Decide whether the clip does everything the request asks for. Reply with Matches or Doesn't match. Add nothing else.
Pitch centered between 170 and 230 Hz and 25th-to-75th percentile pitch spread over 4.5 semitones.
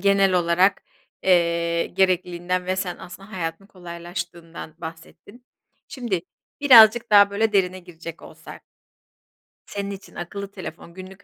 Doesn't match